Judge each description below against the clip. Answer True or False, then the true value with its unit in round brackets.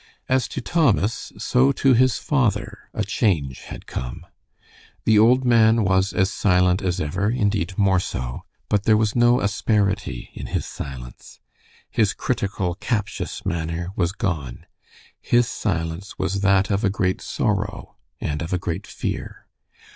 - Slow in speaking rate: False (145 wpm)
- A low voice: True (100 Hz)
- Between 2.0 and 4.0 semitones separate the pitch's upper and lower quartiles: True (3.7 semitones)